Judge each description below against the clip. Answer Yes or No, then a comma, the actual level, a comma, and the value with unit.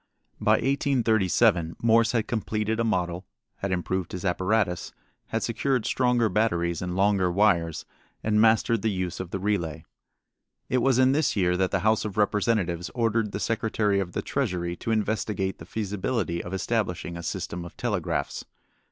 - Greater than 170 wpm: No, average, 160 wpm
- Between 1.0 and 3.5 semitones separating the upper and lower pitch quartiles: No, average, 4.0 semitones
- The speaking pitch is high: No, low, 105 Hz